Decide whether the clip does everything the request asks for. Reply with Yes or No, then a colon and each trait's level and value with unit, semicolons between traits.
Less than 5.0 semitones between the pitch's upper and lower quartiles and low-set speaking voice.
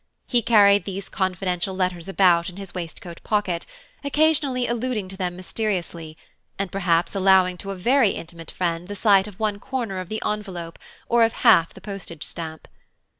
No: average, 3.2 semitones; high, 190 Hz